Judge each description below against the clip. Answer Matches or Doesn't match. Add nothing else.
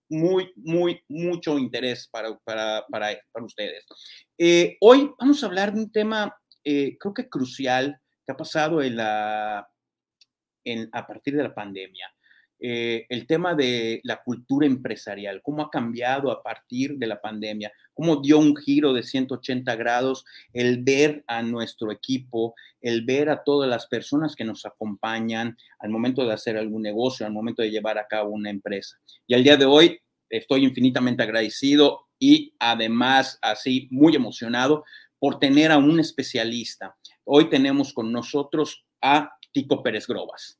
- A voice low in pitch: Matches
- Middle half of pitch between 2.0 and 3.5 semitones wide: Doesn't match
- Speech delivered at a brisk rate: Doesn't match